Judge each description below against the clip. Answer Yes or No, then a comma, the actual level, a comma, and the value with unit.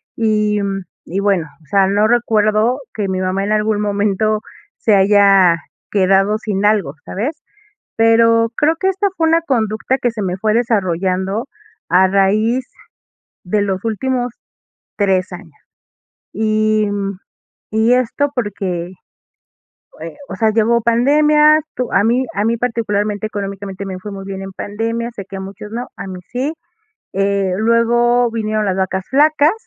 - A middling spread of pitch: Yes, average, 3.0 semitones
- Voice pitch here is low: No, high, 210 Hz